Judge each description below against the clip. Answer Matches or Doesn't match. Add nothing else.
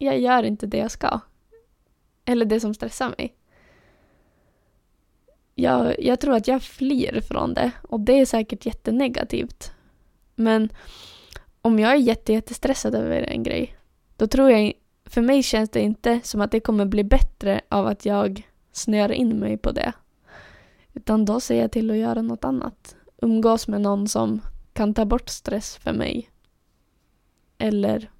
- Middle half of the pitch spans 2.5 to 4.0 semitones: Matches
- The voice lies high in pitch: Matches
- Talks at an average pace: Matches